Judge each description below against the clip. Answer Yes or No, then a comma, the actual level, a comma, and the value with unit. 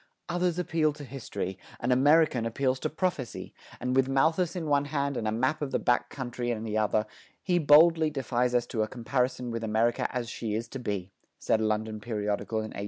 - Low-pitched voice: Yes, low, 125 Hz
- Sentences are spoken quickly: Yes, fast, 210 wpm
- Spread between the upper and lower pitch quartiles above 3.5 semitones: Yes, average, 4.6 semitones